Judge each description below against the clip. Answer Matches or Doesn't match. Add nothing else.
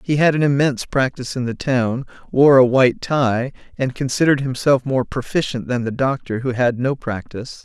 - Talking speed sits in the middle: Matches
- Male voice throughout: Matches